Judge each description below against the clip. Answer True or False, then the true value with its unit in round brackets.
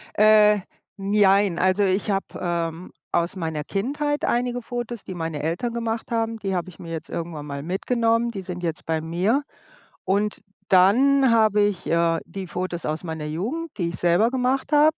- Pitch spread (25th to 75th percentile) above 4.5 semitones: True (5.2 semitones)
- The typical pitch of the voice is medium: False (195 Hz)